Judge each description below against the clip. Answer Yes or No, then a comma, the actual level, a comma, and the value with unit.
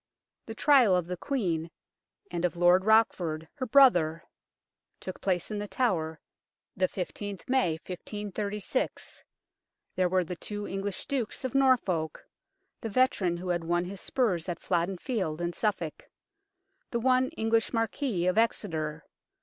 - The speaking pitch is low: No, high, 190 Hz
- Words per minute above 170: No, average, 140 wpm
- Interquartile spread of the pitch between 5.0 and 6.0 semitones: No, average, 4.6 semitones